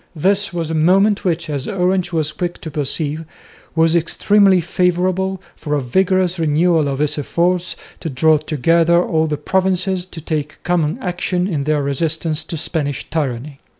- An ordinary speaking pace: Yes, average, 160 wpm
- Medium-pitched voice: Yes, medium, 165 Hz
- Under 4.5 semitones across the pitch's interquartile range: Yes, average, 3.0 semitones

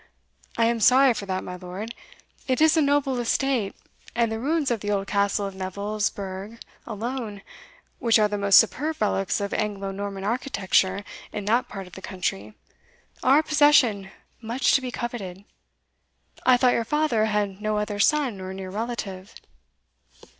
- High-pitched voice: Yes, high, 215 Hz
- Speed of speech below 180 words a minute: Yes, average, 170 wpm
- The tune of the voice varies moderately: Yes, average, 4.1 semitones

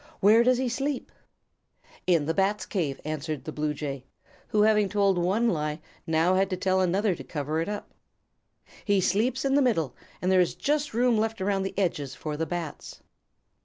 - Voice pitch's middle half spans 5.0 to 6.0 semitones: Yes, average, 5.3 semitones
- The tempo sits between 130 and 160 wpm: No, average, 190 wpm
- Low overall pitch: No, high, 190 Hz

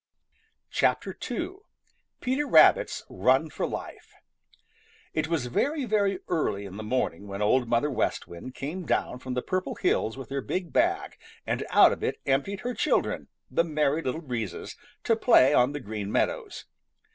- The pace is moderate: Yes, average, 160 wpm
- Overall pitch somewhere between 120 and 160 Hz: Yes, medium, 140 Hz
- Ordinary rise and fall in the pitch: No, wide, 7.3 semitones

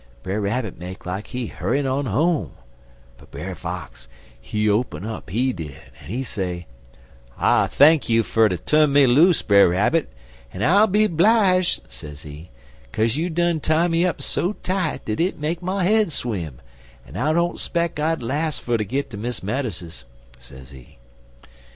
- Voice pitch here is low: Yes, low, 125 Hz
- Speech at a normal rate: Yes, average, 170 wpm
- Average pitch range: No, wide, 8.8 semitones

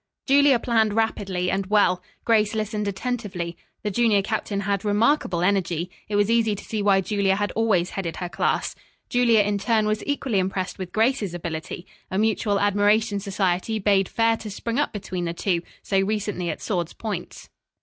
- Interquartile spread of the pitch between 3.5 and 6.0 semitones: No, average, 2.7 semitones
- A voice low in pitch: No, high, 205 Hz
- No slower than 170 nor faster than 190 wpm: Yes, average, 175 wpm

